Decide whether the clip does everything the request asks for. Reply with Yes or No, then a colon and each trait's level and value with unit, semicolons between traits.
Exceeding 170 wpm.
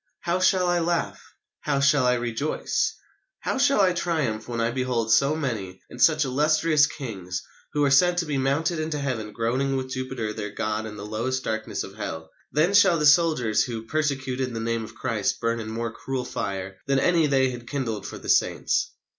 Yes: average, 195 wpm